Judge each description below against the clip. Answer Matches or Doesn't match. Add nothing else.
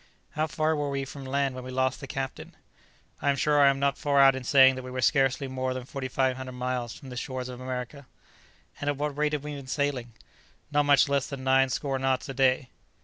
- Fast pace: Matches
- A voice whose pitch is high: Doesn't match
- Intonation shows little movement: Matches